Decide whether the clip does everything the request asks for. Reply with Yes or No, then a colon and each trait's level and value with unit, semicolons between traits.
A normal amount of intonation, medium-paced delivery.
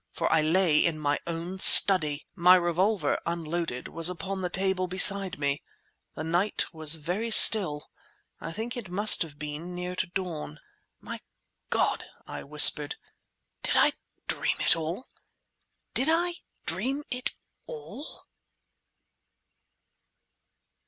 No: average, 3.8 semitones; slow, 125 wpm